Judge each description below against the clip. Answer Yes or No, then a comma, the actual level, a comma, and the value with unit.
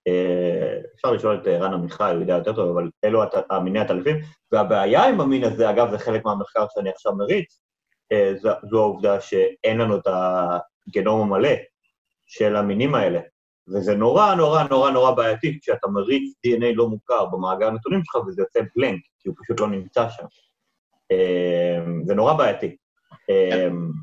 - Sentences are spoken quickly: Yes, fast, 170 wpm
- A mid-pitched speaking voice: No, low, 120 Hz